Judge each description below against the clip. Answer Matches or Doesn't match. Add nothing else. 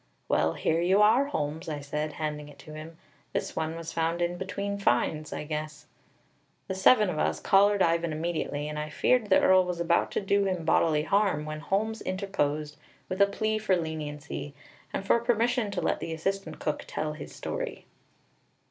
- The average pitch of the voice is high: Doesn't match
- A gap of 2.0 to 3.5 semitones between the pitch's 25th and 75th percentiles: Doesn't match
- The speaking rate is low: Doesn't match